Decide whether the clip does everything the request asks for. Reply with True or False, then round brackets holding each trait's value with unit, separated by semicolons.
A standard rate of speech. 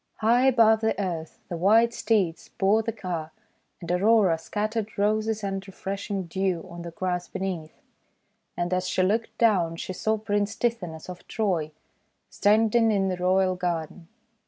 True (160 wpm)